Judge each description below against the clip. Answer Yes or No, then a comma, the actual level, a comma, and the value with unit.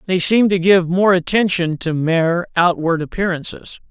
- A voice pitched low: No, medium, 175 Hz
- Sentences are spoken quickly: No, average, 155 wpm